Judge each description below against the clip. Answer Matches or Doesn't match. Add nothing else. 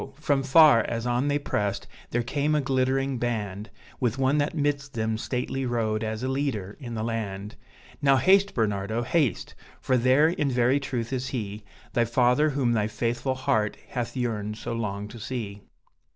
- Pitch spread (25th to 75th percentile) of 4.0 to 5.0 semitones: Doesn't match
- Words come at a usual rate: Matches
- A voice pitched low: Matches